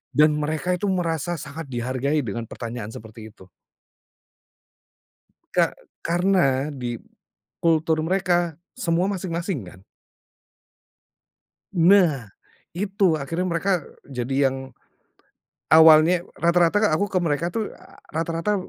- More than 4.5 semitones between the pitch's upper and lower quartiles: Yes, average, 4.9 semitones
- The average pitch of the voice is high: No, medium, 165 Hz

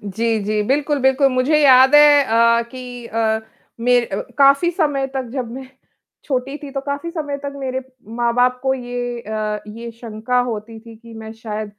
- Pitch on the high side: Yes, very high, 250 Hz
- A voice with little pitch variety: No, average, 3.2 semitones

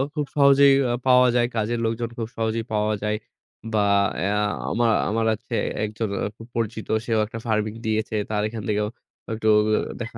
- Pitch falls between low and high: No, low, 110 Hz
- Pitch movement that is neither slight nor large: No, narrow, 1.6 semitones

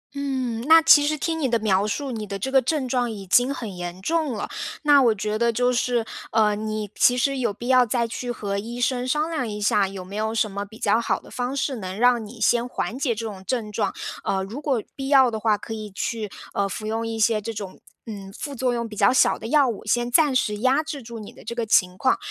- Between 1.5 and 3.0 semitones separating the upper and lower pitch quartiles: No, average, 3.5 semitones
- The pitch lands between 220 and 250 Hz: Yes, high, 230 Hz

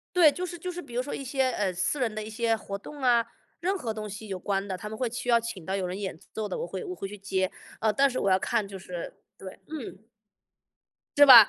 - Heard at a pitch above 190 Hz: Yes, high, 220 Hz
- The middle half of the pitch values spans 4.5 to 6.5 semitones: Yes, average, 5.3 semitones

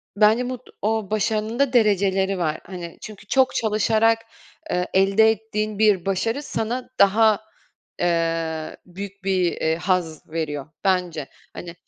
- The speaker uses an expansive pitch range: No, average, 3.8 semitones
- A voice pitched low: No, high, 195 Hz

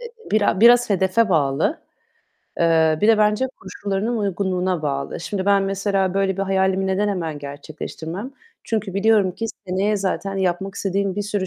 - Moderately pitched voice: No, high, 195 Hz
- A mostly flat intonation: Yes, narrow, 2.3 semitones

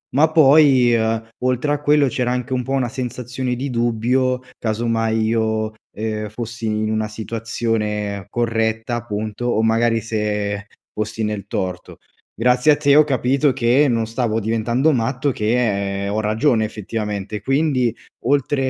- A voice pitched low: Yes, low, 115 Hz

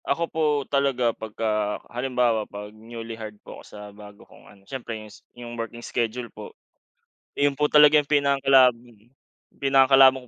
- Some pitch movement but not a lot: Yes, average, 3.6 semitones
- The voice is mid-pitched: No, low, 120 Hz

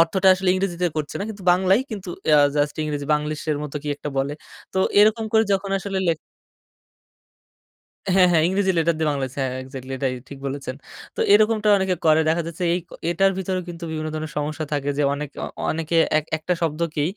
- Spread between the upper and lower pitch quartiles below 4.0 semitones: No, average, 4.3 semitones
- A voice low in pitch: No, medium, 165 Hz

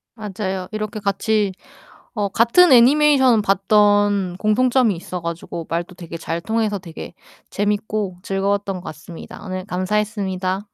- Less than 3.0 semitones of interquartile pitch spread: Yes, narrow, 2.6 semitones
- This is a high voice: Yes, high, 200 Hz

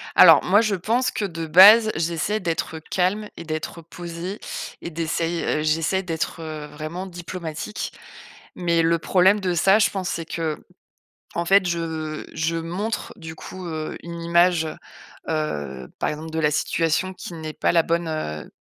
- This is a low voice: No, medium, 170 Hz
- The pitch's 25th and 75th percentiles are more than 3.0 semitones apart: No, narrow, 2.6 semitones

